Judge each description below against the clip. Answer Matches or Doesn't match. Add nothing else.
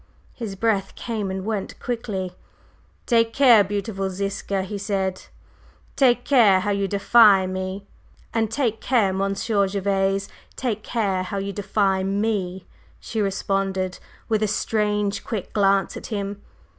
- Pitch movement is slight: Matches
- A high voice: Matches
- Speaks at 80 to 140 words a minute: Matches